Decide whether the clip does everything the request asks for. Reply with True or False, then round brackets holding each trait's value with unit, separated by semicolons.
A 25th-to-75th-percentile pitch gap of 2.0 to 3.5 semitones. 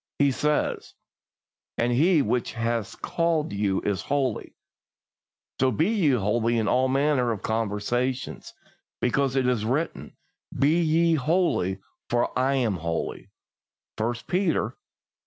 False (4.9 semitones)